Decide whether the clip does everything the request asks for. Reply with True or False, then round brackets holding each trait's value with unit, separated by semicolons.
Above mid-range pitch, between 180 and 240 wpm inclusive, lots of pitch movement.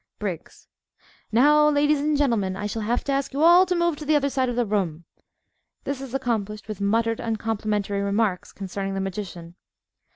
True (225 Hz; 190 wpm; 5.8 semitones)